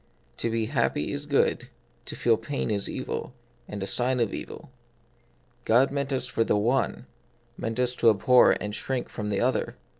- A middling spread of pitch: Yes, average, 3.0 semitones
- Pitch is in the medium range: No, low, 120 Hz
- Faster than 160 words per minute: Yes, average, 180 wpm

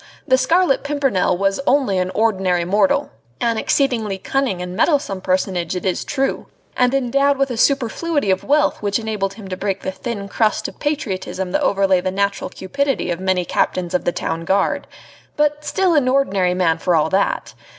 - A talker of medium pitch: No, high, 200 Hz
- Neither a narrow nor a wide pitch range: No, wide, 6.6 semitones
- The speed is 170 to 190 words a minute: Yes, average, 180 wpm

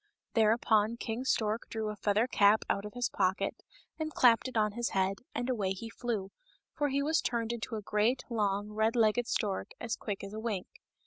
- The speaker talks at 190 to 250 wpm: Yes, average, 200 wpm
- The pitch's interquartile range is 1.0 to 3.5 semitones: Yes, narrow, 2.5 semitones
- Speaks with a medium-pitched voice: No, high, 220 Hz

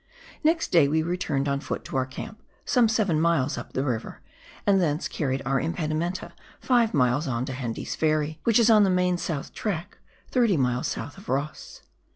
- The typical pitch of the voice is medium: Yes, medium, 155 Hz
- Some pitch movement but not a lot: No, wide, 6.1 semitones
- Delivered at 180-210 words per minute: Yes, average, 190 wpm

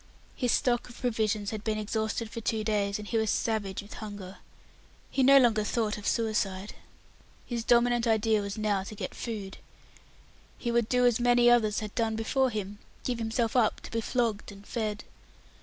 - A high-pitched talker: Yes, high, 220 Hz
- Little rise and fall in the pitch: Yes, narrow, 2.2 semitones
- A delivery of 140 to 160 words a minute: No, average, 185 wpm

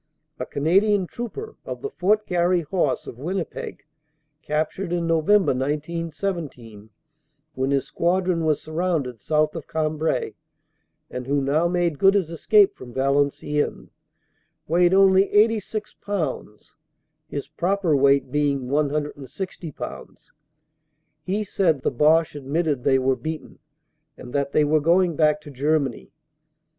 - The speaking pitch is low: No, medium, 155 Hz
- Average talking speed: No, slow, 130 wpm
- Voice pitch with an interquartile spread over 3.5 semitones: Yes, average, 4.5 semitones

